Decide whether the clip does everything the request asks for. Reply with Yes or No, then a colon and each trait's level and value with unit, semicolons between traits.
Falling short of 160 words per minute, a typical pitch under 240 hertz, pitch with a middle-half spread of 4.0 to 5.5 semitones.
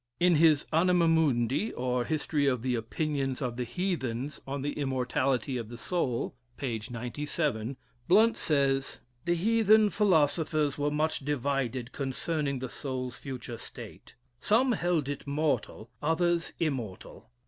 Yes: slow, 135 wpm; medium, 140 Hz; average, 4.4 semitones